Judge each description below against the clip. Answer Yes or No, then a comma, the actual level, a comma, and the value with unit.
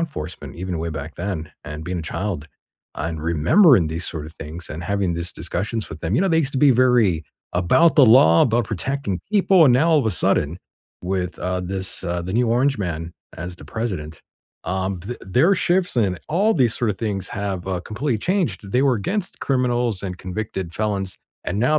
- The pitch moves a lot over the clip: Yes, wide, 6.5 semitones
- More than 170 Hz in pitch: No, very low, 95 Hz